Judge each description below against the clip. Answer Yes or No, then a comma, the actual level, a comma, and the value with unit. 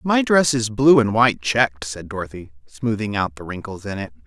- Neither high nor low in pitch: No, low, 110 Hz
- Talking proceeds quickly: Yes, fast, 210 wpm